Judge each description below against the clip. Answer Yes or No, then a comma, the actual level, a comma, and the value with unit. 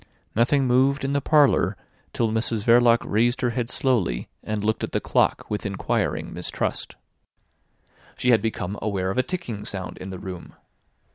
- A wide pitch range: No, average, 3.8 semitones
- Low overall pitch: Yes, low, 115 Hz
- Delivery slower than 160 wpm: No, average, 165 wpm